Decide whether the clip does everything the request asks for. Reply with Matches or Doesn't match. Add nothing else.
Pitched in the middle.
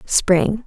Doesn't match